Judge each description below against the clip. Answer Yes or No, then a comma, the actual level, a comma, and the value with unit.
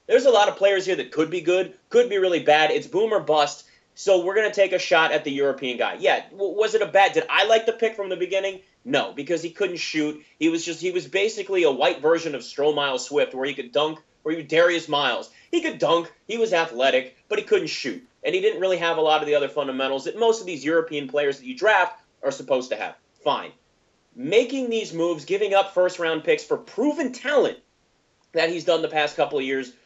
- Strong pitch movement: Yes, wide, 7.6 semitones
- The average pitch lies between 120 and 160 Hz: No, medium, 180 Hz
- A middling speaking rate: No, fast, 245 wpm